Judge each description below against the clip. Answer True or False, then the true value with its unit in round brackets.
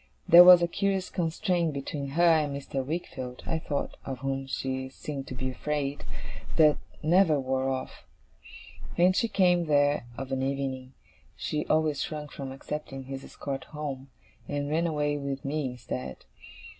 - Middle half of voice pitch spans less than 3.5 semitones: True (2.9 semitones)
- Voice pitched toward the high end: False (145 Hz)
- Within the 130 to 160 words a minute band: True (155 wpm)